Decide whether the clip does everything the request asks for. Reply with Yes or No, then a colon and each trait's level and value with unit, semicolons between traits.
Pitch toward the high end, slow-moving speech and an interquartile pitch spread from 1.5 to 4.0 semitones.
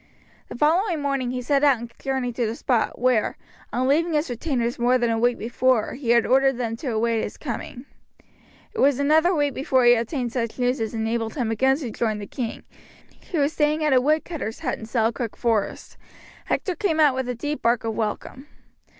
No: very high, 250 Hz; fast, 205 wpm; average, 3.6 semitones